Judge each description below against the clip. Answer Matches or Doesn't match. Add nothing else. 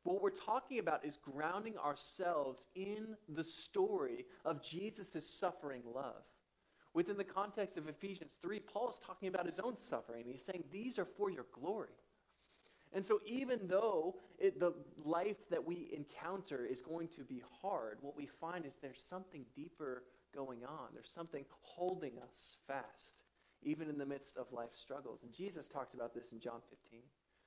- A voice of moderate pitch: Matches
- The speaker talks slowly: Doesn't match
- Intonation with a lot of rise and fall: Matches